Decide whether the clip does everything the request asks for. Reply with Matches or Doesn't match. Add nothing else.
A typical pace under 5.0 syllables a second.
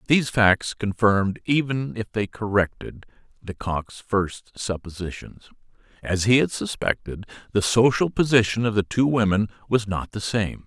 Matches